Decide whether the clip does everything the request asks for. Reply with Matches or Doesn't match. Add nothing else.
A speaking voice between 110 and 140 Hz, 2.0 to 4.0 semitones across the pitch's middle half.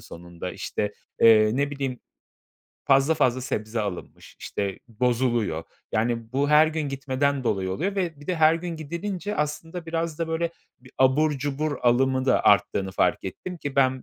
Doesn't match